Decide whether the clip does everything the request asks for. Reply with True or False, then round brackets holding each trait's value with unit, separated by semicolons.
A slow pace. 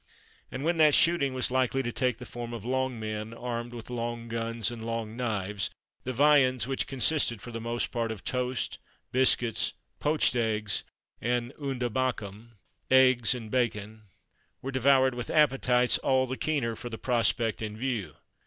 False (165 wpm)